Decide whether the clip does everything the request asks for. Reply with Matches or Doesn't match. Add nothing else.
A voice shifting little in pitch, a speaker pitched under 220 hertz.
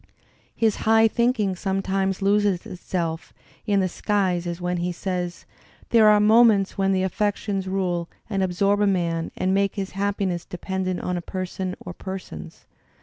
Matches